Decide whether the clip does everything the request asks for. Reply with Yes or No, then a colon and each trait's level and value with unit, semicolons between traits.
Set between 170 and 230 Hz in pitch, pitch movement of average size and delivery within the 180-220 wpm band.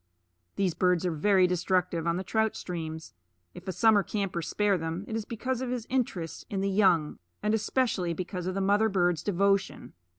Yes: high, 190 Hz; average, 3.1 semitones; average, 190 wpm